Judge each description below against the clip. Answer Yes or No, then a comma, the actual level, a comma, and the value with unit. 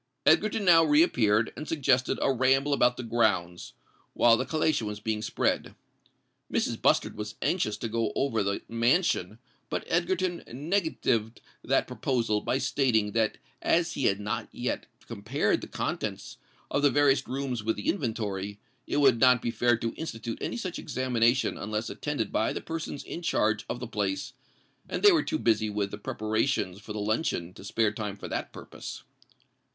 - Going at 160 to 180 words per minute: Yes, average, 175 wpm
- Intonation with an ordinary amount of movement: Yes, average, 5.0 semitones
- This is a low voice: Yes, low, 120 Hz